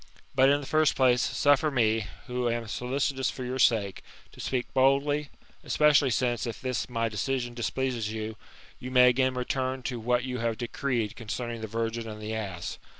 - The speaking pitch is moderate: No, low, 125 Hz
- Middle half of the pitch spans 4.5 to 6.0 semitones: No, narrow, 2.6 semitones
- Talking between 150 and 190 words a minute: Yes, average, 180 wpm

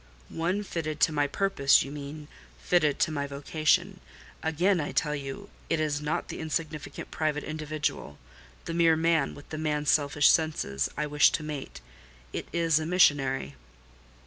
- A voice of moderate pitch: Yes, medium, 150 Hz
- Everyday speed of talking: Yes, average, 145 wpm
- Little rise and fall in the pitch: Yes, narrow, 1.9 semitones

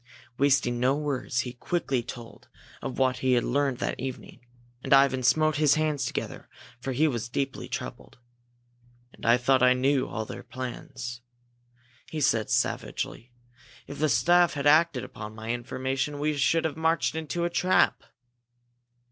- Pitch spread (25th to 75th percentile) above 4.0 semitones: No, average, 3.5 semitones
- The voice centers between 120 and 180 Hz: Yes, low, 135 Hz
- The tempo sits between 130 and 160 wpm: Yes, average, 155 wpm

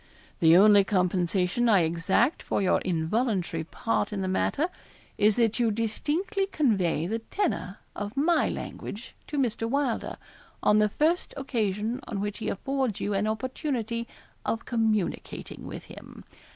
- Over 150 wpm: No, average, 145 wpm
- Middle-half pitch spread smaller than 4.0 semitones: No, average, 4.6 semitones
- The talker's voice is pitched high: Yes, high, 220 Hz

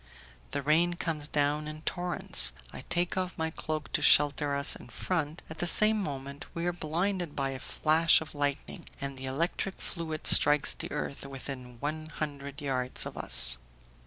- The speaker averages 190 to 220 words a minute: No, average, 175 wpm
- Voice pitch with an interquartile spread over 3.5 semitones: No, average, 3.2 semitones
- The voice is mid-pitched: Yes, medium, 150 Hz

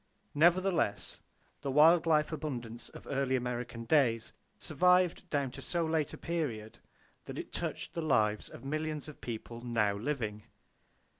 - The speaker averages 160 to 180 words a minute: No, average, 145 wpm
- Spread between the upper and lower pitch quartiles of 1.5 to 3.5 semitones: No, average, 5.2 semitones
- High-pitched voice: No, medium, 140 Hz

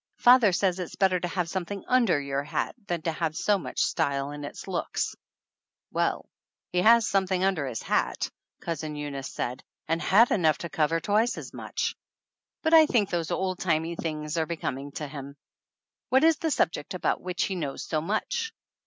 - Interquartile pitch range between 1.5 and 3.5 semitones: No, average, 4.5 semitones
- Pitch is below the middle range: No, medium, 170 Hz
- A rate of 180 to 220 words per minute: Yes, average, 190 wpm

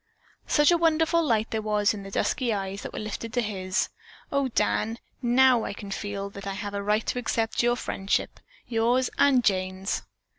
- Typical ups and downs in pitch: Yes, average, 3.7 semitones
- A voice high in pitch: Yes, high, 220 Hz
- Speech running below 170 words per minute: No, average, 190 wpm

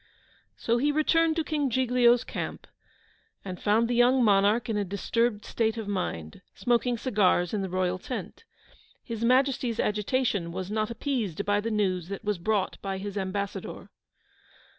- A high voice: Yes, high, 215 Hz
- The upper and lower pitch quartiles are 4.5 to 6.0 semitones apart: No, average, 3.7 semitones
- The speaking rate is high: No, average, 160 wpm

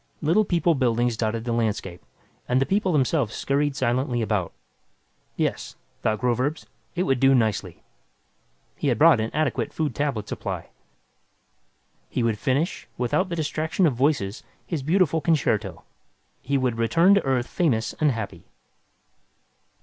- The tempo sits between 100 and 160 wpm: Yes, average, 140 wpm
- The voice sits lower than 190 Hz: Yes, low, 135 Hz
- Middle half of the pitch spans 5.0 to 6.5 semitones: Yes, average, 5.3 semitones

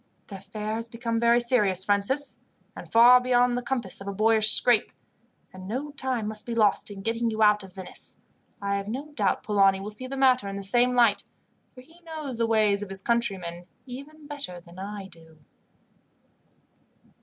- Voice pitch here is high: Yes, high, 220 Hz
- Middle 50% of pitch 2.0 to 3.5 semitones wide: No, average, 3.9 semitones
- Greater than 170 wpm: Yes, average, 190 wpm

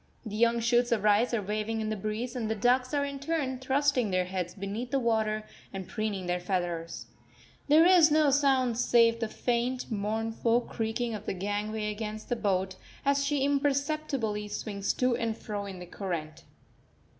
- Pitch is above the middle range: Yes, high, 225 Hz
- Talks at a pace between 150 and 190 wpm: Yes, average, 180 wpm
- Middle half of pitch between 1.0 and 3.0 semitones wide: No, average, 3.8 semitones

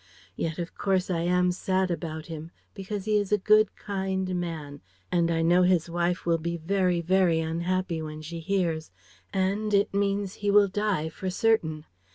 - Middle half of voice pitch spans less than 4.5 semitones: Yes, average, 2.9 semitones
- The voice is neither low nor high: Yes, medium, 180 Hz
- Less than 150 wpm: No, average, 180 wpm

